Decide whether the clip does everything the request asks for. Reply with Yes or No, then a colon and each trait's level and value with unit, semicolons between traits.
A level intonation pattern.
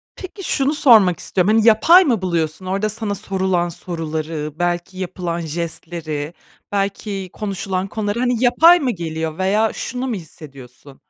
No: average, 4.9 semitones